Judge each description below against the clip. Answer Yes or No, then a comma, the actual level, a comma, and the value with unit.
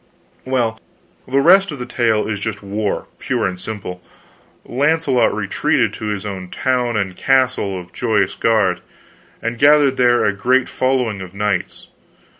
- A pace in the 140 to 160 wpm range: Yes, average, 145 wpm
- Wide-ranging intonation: No, average, 4.4 semitones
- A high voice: No, low, 115 Hz